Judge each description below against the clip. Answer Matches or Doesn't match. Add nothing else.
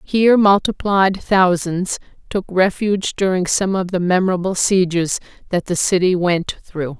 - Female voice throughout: Matches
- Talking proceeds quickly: Doesn't match